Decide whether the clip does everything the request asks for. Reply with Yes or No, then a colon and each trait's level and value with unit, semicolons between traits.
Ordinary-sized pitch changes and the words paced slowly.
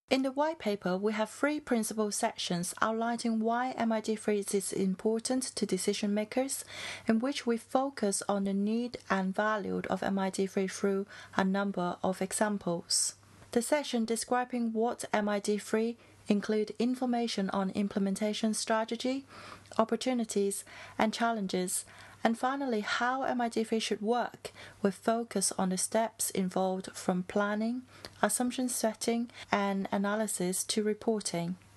Yes: average, 3.0 semitones; slow, 125 wpm